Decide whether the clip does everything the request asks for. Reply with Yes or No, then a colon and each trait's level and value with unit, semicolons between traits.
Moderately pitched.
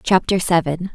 Yes: medium, 175 Hz